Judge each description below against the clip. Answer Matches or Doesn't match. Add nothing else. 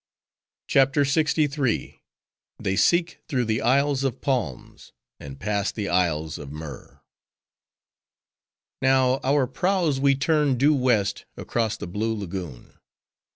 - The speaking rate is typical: Doesn't match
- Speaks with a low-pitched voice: Matches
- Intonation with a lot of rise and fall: Matches